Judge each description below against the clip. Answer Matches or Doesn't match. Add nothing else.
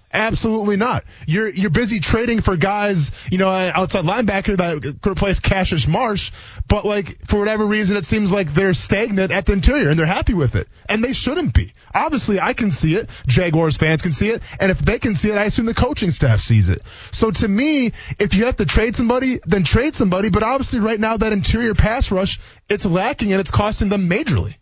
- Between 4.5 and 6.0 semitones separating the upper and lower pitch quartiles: Matches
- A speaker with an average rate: Doesn't match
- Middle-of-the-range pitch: Doesn't match